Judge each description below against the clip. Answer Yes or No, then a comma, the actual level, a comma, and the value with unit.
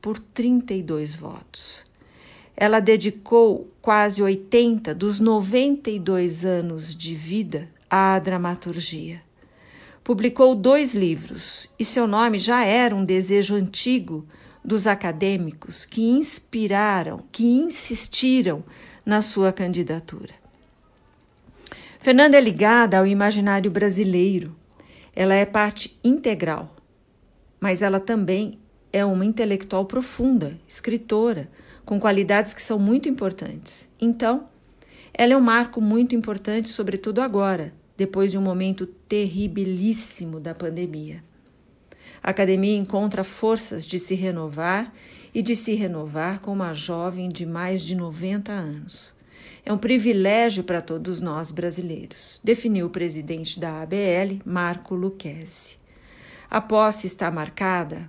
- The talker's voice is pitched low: No, high, 195 Hz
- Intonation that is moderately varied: Yes, average, 3.9 semitones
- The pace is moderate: No, slow, 115 wpm